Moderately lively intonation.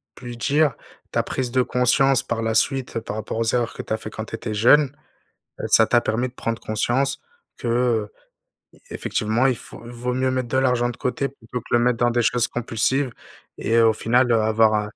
No: narrow, 2.2 semitones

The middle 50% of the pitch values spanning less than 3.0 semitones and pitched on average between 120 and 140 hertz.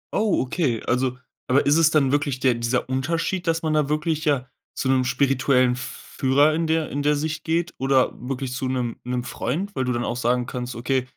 No: average, 3.4 semitones; low, 135 Hz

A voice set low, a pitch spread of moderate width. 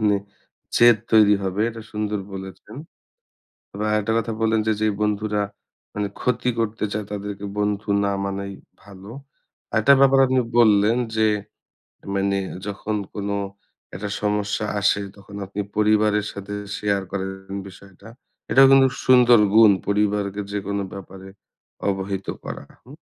No: low, 105 Hz; narrow, 1.5 semitones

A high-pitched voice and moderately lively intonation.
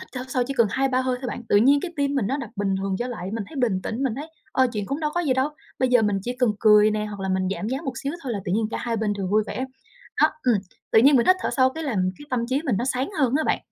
Yes: very high, 250 Hz; average, 4.3 semitones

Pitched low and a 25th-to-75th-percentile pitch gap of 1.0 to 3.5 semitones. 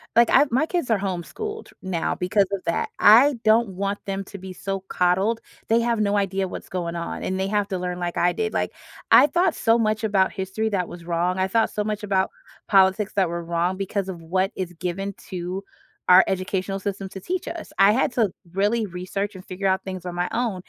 No: high, 195 Hz; average, 2.8 semitones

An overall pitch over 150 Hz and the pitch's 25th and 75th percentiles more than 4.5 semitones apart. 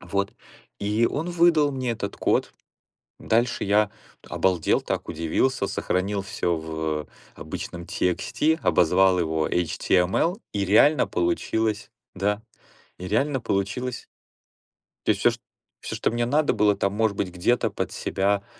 No: low, 100 Hz; average, 5.1 semitones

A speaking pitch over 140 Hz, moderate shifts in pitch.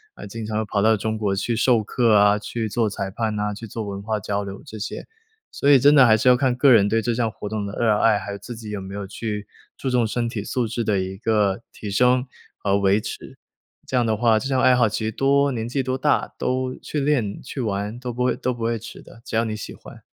No: low, 110 Hz; average, 3.2 semitones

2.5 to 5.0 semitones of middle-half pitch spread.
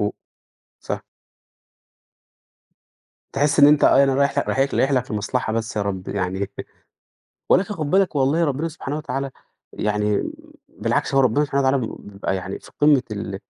No: wide, 5.5 semitones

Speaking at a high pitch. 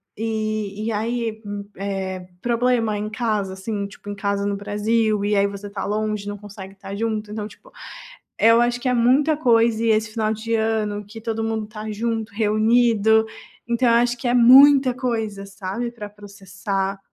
Yes: high, 215 Hz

